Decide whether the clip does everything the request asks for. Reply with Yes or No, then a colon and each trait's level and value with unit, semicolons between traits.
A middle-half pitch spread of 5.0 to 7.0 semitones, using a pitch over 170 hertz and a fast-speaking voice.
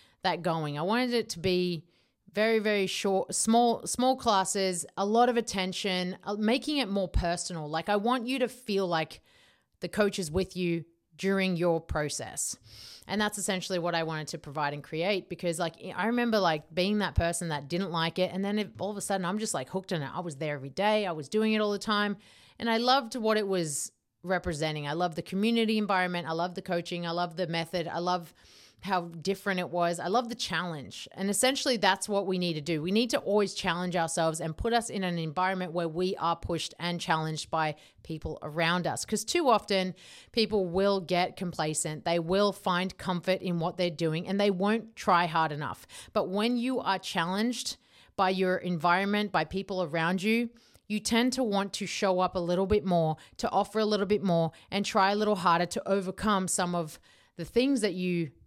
No: average, 3.4 semitones; medium, 185 Hz; fast, 210 wpm